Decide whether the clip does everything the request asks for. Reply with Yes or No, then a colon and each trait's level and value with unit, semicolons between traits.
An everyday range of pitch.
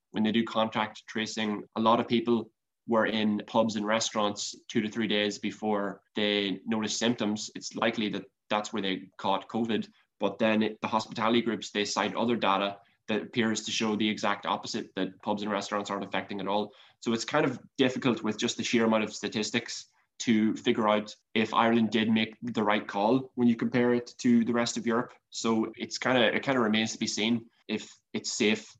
No: narrow, 1.8 semitones